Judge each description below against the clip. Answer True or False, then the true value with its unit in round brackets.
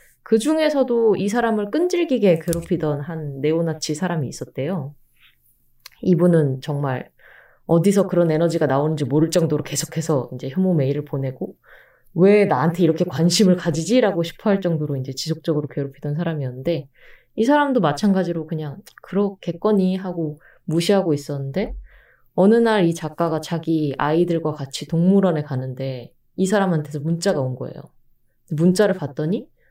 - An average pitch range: True (4.3 semitones)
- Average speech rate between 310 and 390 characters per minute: True (345 characters per minute)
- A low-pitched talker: False (165 Hz)